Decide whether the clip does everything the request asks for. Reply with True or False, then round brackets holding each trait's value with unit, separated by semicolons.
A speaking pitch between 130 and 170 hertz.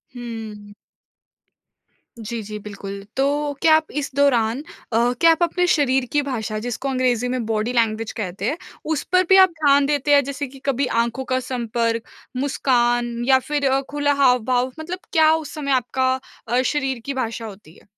False (255 Hz)